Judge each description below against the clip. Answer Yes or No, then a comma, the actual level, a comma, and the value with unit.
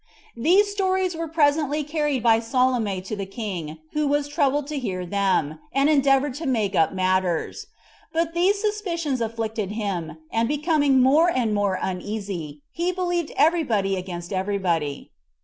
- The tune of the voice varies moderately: No, wide, 7.9 semitones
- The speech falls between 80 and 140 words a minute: No, average, 155 wpm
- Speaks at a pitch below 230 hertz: No, very high, 250 Hz